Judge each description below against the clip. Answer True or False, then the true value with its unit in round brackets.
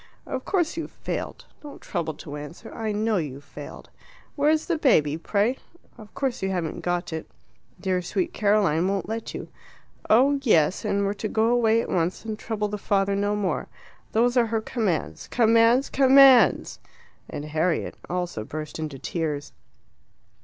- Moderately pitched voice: False (210 Hz)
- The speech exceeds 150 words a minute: True (160 wpm)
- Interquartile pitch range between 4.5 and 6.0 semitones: True (5.5 semitones)